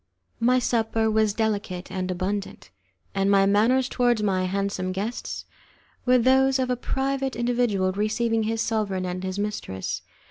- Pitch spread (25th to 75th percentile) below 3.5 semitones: No, average, 3.9 semitones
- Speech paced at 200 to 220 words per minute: No, average, 145 wpm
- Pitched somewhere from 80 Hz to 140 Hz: No, high, 215 Hz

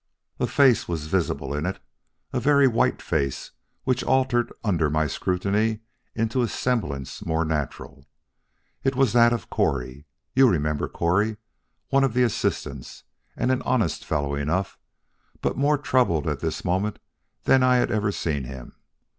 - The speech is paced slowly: No, average, 155 wpm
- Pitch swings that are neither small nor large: No, wide, 8.8 semitones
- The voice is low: Yes, low, 100 Hz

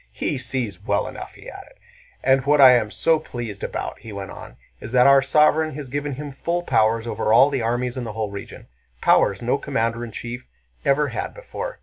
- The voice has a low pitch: Yes, low, 125 Hz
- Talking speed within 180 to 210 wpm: Yes, fast, 205 wpm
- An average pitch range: Yes, average, 4.2 semitones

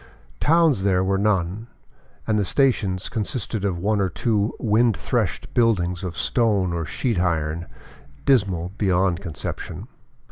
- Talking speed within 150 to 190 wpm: No, slow, 135 wpm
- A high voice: No, low, 100 Hz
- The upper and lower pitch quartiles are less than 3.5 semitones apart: No, average, 3.8 semitones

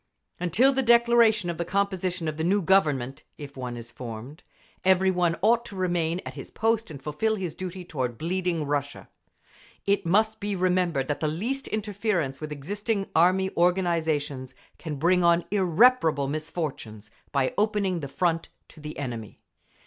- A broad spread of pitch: No, average, 5.0 semitones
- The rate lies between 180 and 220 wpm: No, average, 155 wpm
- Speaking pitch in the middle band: Yes, medium, 175 Hz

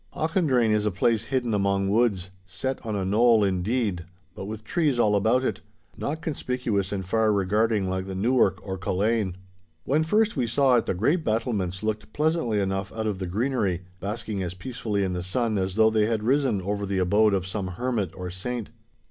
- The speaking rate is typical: Yes, average, 190 wpm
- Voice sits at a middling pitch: No, low, 105 Hz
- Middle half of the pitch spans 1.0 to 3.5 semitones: No, average, 4.0 semitones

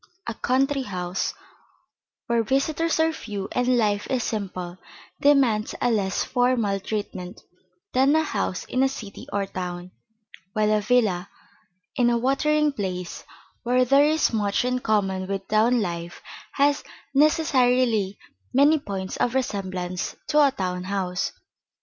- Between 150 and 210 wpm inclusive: No, slow, 135 wpm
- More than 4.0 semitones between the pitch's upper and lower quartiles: Yes, wide, 5.6 semitones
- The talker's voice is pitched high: Yes, high, 225 Hz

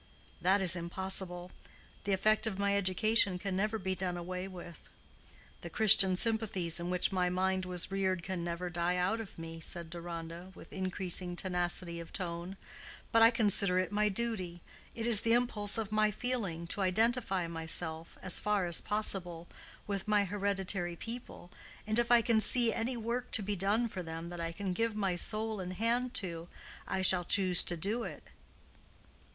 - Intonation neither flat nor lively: Yes, average, 3.4 semitones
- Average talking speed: Yes, average, 175 wpm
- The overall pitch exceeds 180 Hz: Yes, high, 190 Hz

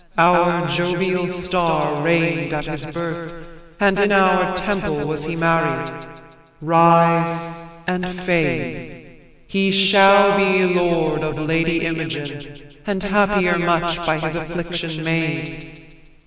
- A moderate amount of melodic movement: No, narrow, 2.1 semitones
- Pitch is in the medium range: Yes, medium, 170 Hz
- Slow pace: Yes, slow, 115 wpm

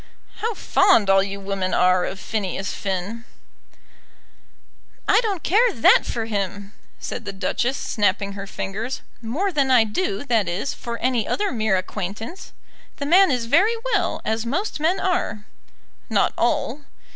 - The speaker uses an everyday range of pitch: No, wide, 8.0 semitones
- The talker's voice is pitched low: No, high, 230 Hz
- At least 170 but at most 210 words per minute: No, average, 150 wpm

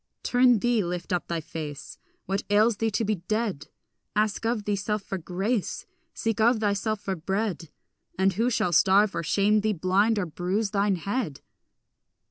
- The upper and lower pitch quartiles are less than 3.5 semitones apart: Yes, average, 3.0 semitones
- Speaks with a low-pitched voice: No, high, 205 Hz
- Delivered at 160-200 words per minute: Yes, average, 165 wpm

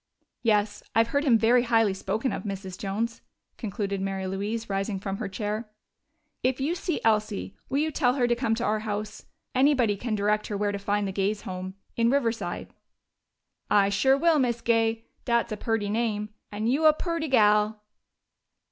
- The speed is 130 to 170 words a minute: No, average, 180 wpm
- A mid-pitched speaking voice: No, high, 220 Hz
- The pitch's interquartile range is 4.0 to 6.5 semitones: No, average, 2.8 semitones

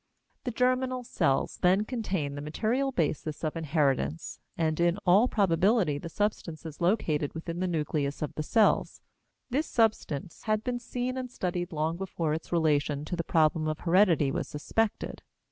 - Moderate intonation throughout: No, wide, 5.8 semitones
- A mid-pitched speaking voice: Yes, medium, 170 Hz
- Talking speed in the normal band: Yes, average, 160 wpm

